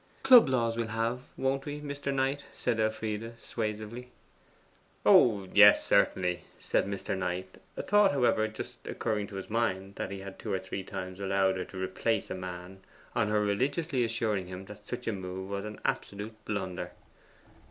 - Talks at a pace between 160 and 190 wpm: Yes, average, 175 wpm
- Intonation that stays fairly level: No, average, 3.7 semitones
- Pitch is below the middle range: Yes, low, 105 Hz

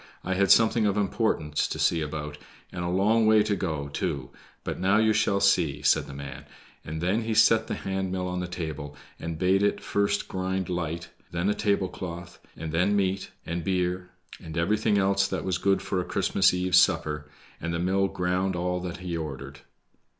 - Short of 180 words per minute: No, average, 200 wpm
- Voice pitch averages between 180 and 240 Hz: No, very low, 90 Hz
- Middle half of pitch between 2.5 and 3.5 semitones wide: Yes, average, 2.9 semitones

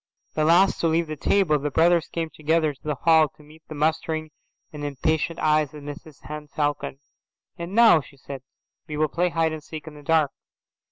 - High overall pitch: No, medium, 155 Hz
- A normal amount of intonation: No, narrow, 1.6 semitones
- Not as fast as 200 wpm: No, fast, 205 wpm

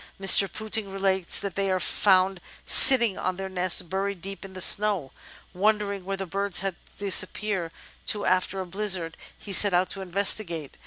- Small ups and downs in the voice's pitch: Yes, narrow, 1.5 semitones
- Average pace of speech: Yes, average, 170 wpm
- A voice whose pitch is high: Yes, high, 195 Hz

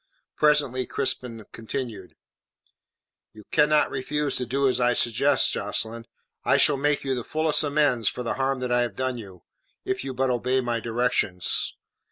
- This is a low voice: Yes, low, 125 Hz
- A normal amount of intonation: Yes, average, 3.0 semitones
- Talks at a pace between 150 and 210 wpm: Yes, average, 165 wpm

